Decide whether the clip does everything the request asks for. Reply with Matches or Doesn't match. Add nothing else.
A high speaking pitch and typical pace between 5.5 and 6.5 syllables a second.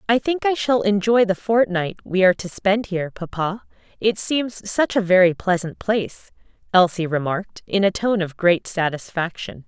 Doesn't match